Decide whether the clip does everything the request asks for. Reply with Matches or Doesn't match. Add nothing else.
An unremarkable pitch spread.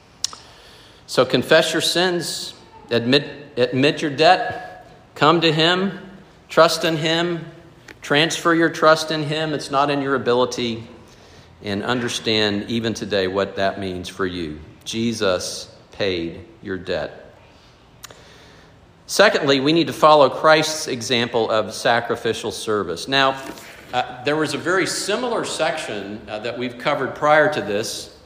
Doesn't match